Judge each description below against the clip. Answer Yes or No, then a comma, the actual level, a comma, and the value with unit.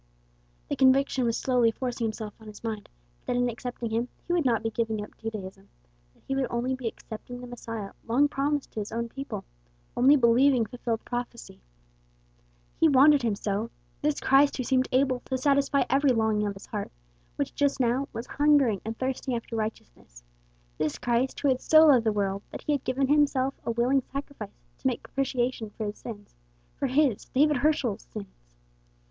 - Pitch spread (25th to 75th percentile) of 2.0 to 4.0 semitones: Yes, average, 3.5 semitones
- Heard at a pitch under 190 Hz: No, high, 245 Hz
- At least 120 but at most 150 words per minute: No, average, 185 wpm